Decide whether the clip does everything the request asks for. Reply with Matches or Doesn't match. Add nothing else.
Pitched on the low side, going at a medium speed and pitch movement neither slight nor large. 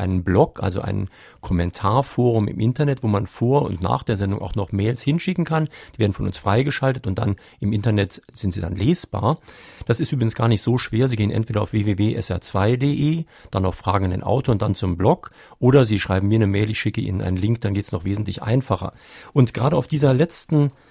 Doesn't match